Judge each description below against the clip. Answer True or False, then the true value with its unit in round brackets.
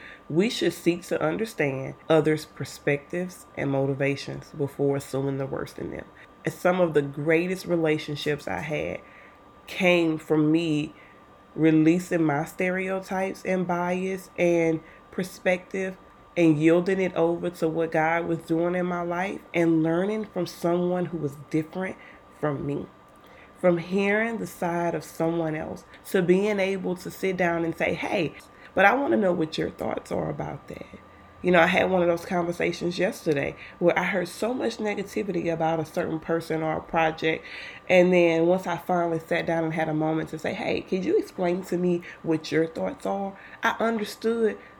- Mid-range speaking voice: True (170 Hz)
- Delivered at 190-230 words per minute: False (170 wpm)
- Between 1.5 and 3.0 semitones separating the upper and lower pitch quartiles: True (2.6 semitones)